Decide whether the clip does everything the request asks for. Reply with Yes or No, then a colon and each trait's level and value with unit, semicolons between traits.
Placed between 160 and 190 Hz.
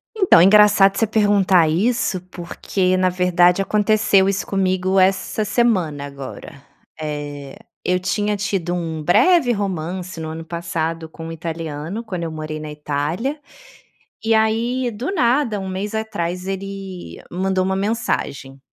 Yes: medium, 185 Hz